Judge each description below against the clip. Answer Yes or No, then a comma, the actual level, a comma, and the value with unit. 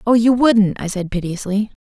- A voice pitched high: Yes, high, 210 Hz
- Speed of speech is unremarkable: Yes, average, 195 wpm